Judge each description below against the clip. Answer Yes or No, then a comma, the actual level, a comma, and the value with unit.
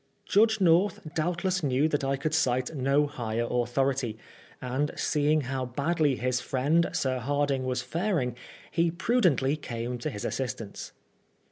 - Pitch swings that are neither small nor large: Yes, average, 4.0 semitones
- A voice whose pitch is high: No, medium, 140 Hz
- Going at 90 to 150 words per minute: Yes, average, 140 wpm